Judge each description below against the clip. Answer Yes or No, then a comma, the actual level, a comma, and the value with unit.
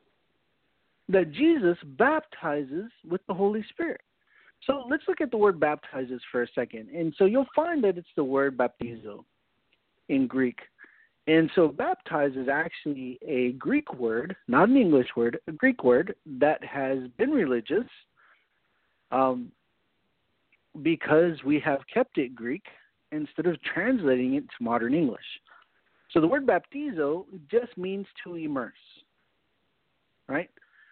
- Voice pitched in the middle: Yes, medium, 165 Hz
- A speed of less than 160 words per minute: Yes, slow, 135 wpm